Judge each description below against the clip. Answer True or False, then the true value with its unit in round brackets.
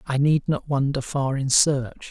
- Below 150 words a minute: False (200 wpm)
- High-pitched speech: False (140 Hz)